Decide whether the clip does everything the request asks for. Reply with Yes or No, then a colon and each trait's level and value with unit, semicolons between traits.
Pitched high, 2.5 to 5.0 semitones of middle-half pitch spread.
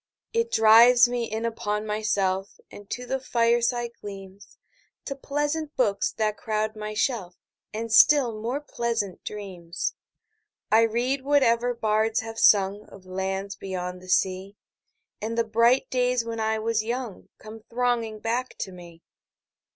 Yes: high, 220 Hz; average, 3.0 semitones